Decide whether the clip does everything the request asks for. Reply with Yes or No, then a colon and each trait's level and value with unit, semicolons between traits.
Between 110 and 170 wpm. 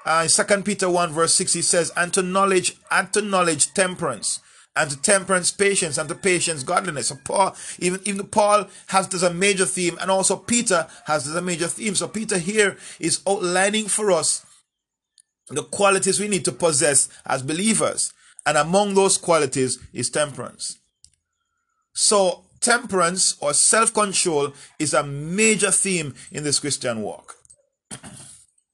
Yes: average, 155 wpm